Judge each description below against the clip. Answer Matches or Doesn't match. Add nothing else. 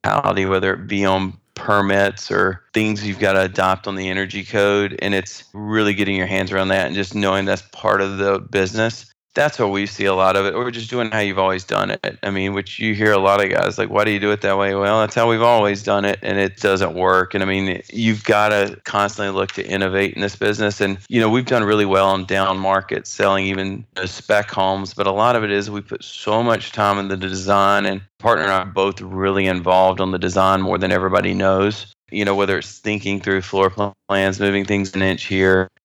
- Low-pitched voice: Matches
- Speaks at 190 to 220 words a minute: Doesn't match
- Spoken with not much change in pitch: Matches